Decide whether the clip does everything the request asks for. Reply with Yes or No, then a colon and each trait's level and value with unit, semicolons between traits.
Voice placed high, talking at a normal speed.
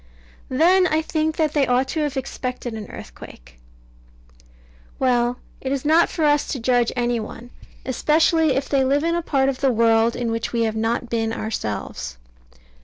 Yes: very high, 255 Hz; average, 180 wpm